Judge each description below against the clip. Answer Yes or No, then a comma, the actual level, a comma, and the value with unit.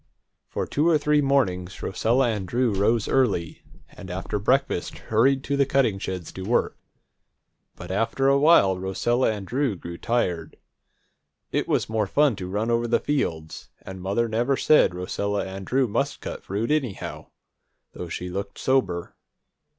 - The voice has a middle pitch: No, low, 110 Hz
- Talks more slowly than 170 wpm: Yes, average, 160 wpm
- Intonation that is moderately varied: No, wide, 5.9 semitones